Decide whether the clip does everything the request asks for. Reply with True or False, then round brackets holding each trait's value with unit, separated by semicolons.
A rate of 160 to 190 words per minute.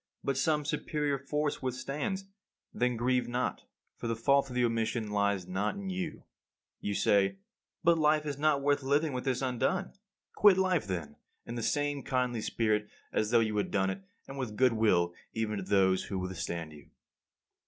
True (170 wpm)